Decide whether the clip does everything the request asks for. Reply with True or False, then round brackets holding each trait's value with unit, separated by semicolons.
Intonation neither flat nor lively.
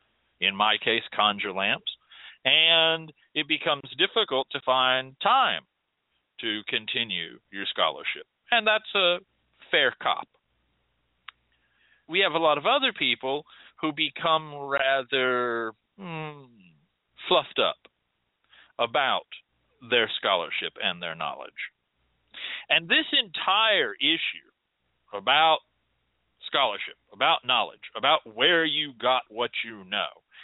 True (4.3 semitones)